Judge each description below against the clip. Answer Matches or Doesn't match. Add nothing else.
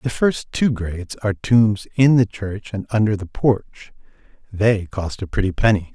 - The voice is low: Matches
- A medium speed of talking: Matches